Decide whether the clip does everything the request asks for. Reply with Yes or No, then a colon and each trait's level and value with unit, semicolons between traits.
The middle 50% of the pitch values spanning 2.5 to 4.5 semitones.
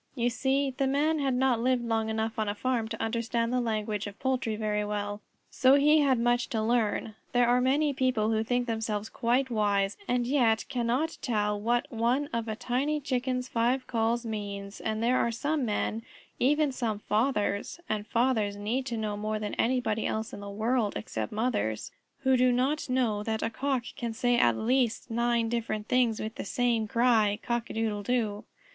Yes: average, 2.8 semitones